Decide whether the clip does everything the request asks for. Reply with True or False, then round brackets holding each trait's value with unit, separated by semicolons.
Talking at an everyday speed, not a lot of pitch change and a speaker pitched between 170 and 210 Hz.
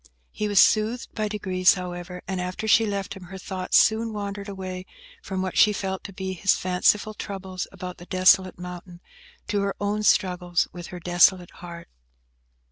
True (175 wpm; 2.1 semitones; 190 Hz)